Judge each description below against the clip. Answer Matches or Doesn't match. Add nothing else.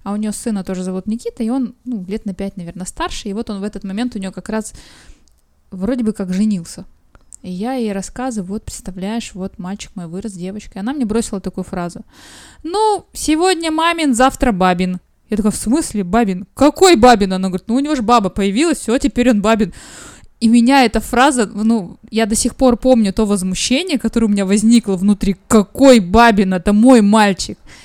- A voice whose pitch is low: Doesn't match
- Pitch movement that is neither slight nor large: Matches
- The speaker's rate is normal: Doesn't match